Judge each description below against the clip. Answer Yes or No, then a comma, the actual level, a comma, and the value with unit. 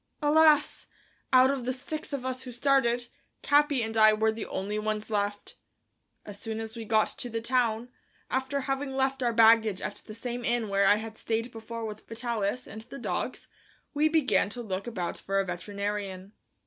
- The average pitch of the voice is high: Yes, high, 230 Hz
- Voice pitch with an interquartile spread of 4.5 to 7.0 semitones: No, average, 3.3 semitones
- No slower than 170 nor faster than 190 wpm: Yes, average, 185 wpm